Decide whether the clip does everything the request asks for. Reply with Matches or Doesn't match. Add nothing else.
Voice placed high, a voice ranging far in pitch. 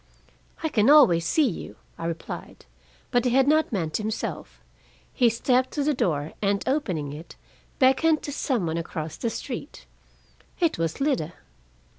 Matches